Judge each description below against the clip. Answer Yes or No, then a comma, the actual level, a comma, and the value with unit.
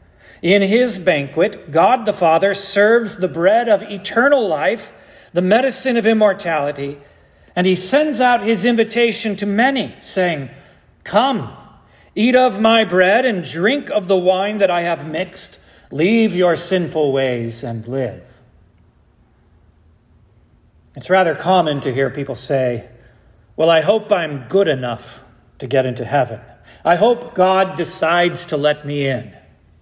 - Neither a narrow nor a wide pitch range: No, wide, 7.6 semitones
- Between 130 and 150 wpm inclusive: Yes, average, 140 wpm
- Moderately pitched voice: Yes, medium, 180 Hz